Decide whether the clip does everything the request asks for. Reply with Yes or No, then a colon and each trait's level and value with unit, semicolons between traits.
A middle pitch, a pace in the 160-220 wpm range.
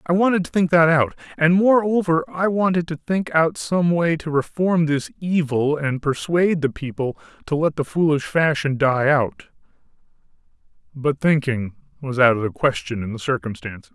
Yes: medium, 150 Hz; average, 170 wpm